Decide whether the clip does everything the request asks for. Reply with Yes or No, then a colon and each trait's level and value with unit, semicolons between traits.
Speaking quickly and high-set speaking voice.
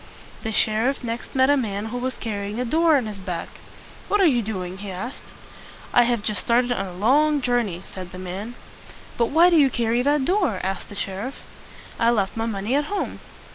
Yes: fast, 215 wpm; high, 230 Hz